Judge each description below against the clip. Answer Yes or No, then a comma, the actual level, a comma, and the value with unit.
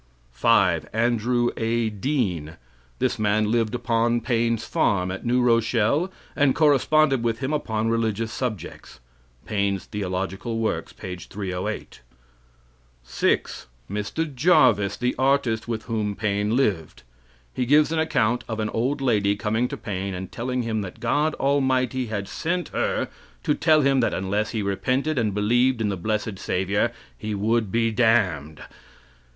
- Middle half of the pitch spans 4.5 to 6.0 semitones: No, average, 3.7 semitones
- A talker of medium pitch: No, low, 115 Hz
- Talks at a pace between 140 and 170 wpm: Yes, average, 145 wpm